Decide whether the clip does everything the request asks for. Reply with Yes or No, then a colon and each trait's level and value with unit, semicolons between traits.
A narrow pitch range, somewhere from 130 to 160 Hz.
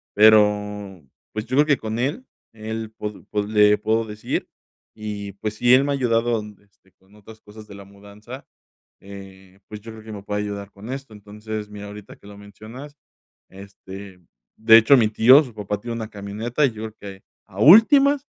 No: narrow, 2.0 semitones; low, 105 Hz